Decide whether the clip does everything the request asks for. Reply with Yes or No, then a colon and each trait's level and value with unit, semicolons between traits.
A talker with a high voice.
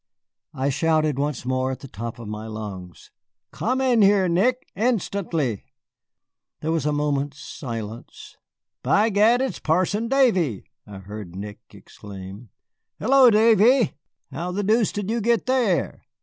No: medium, 160 Hz